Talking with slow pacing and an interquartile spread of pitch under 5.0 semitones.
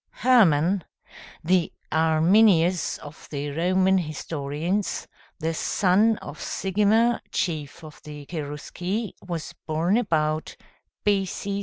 Yes: slow, 105 wpm; average, 4.2 semitones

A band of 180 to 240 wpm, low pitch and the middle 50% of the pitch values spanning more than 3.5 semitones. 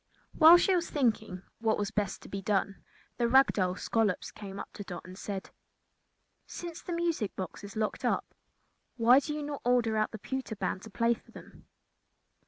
No: average, 190 wpm; high, 220 Hz; average, 5.0 semitones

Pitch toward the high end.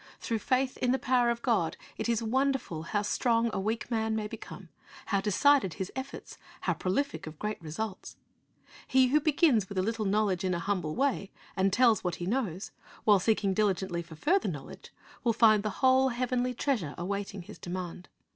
Yes: high, 215 Hz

